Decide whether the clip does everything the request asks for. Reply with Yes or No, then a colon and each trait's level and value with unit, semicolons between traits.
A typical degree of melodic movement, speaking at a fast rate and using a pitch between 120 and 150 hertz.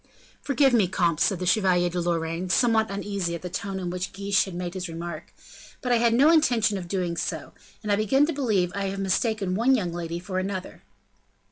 No: average, 3.7 semitones; fast, 220 wpm; high, 190 Hz